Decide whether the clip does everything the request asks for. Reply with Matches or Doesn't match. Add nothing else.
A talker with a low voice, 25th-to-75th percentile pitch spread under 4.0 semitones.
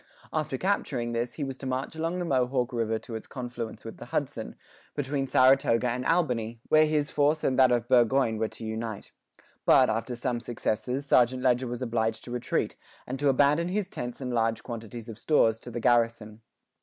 Matches